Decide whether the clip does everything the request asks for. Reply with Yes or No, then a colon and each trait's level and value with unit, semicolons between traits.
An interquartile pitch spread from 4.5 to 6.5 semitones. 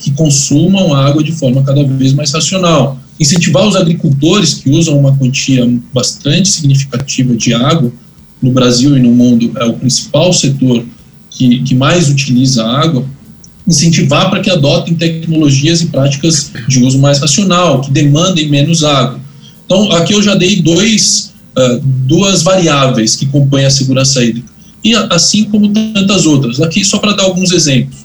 Yes: average, 5.0 semitones